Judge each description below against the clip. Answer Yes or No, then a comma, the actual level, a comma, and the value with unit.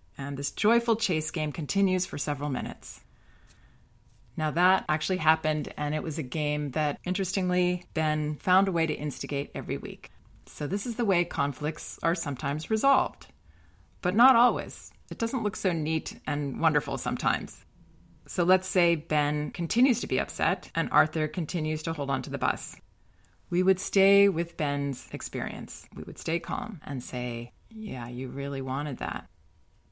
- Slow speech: No, average, 165 wpm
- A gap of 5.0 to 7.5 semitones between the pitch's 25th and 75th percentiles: No, average, 4.6 semitones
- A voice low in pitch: No, medium, 155 Hz